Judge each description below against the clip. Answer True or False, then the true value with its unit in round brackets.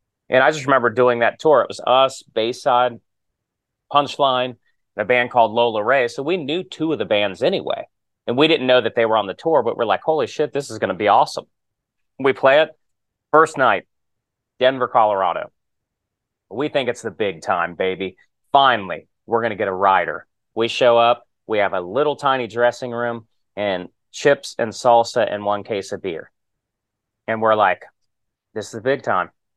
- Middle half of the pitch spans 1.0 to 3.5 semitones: True (2.6 semitones)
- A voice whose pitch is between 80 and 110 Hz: False (120 Hz)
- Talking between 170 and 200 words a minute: True (195 wpm)